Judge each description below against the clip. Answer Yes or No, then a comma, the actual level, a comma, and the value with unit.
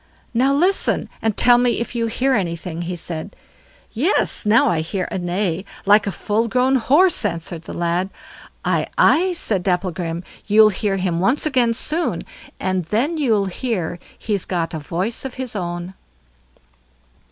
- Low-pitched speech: No, high, 205 Hz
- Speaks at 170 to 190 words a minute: No, average, 160 wpm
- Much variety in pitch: Yes, wide, 5.8 semitones